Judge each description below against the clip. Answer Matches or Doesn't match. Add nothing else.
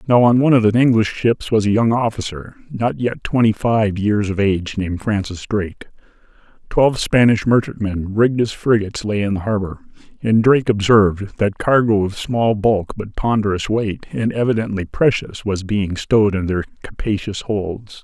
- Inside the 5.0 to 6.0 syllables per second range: Matches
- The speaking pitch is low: Matches